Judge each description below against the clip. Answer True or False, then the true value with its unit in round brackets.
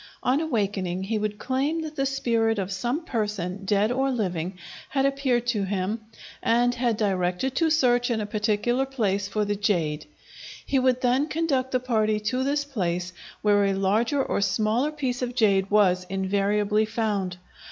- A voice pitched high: True (220 Hz)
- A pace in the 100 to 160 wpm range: False (170 wpm)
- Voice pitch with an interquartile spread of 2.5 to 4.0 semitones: False (4.4 semitones)